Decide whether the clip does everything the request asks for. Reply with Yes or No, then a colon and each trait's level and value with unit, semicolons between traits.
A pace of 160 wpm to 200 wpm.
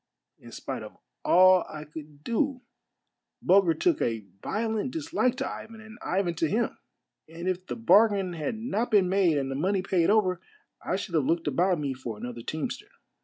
Yes: average, 180 wpm